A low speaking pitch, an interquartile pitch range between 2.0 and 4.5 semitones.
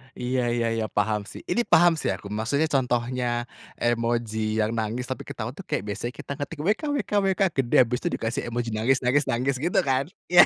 Yes: low, 125 Hz; average, 3.8 semitones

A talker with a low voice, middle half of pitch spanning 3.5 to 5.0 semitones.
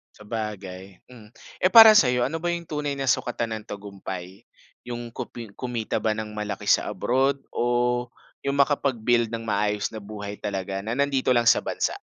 Yes: low, 115 Hz; average, 3.8 semitones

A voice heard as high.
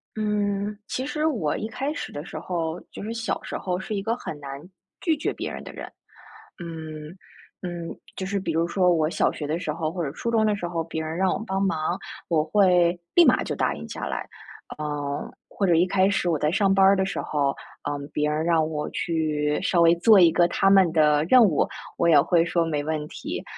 No: medium, 170 Hz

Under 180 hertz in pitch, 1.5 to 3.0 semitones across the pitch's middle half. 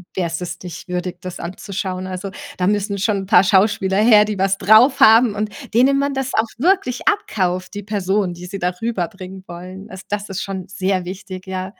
No: high, 195 Hz; narrow, 2.5 semitones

